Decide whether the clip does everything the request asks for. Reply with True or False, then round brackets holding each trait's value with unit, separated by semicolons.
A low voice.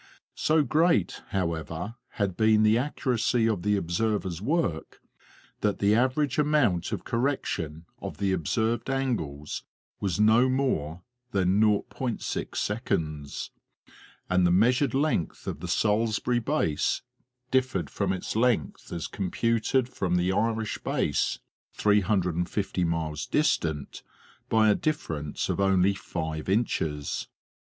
True (105 Hz)